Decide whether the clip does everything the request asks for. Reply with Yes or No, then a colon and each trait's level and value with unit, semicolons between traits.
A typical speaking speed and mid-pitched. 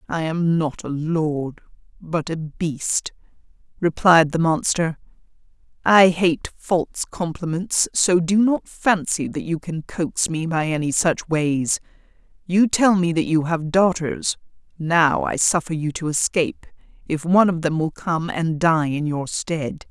Yes: average, 155 wpm; medium, 165 Hz